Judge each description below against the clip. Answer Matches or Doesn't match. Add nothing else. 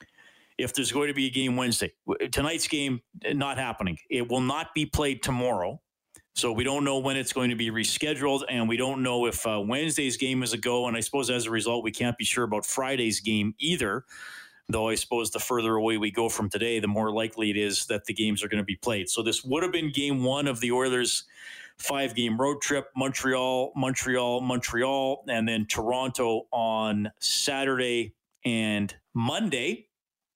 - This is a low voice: Matches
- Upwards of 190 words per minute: Matches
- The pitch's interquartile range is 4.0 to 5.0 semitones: Doesn't match